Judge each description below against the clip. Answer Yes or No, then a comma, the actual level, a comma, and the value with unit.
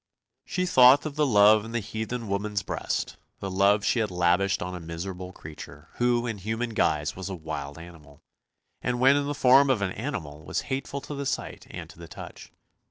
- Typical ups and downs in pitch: No, wide, 5.9 semitones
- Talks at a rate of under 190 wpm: No, fast, 205 wpm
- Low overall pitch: Yes, low, 105 Hz